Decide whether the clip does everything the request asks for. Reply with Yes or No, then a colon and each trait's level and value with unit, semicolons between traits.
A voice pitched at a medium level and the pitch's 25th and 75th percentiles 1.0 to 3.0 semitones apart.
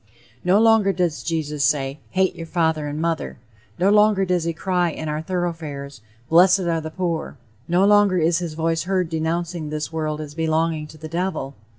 Yes: medium, 165 Hz; average, 2.7 semitones